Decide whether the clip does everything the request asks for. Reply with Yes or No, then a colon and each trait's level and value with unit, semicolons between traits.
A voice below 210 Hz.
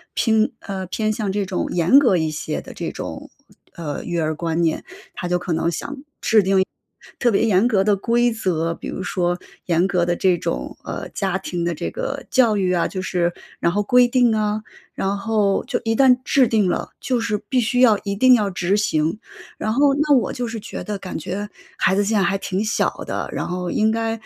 Yes: high, 200 Hz